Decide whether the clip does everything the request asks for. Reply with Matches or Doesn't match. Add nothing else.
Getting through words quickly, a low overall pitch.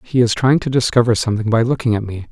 Matches